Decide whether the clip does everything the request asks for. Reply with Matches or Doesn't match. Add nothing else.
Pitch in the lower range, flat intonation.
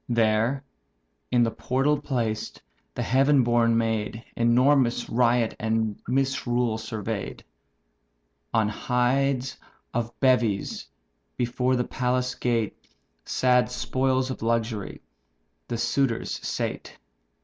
Matches